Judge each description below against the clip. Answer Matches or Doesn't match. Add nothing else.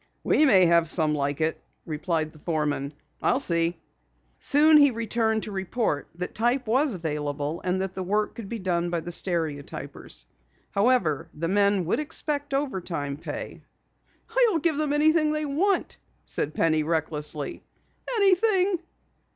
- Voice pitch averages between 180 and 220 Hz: Matches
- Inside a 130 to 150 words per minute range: Matches